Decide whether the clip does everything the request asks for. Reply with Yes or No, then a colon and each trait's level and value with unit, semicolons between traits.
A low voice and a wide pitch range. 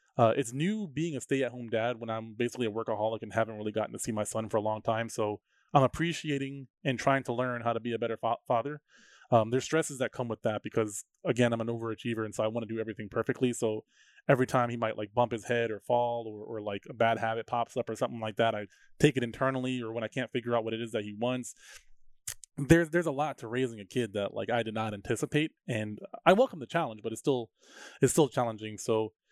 No: low, 120 Hz; average, 3.0 semitones